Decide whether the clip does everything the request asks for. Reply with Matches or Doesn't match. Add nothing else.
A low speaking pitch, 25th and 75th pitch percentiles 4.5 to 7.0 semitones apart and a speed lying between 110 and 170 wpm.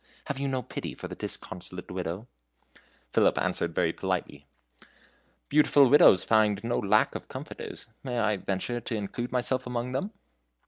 Matches